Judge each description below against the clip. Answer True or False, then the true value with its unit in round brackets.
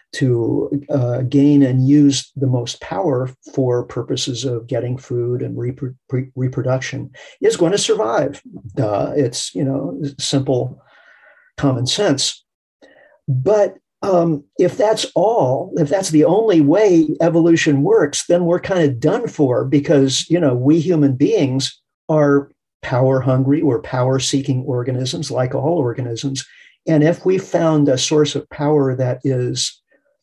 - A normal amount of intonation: True (3.7 semitones)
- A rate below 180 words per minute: True (145 wpm)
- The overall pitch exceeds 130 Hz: True (140 Hz)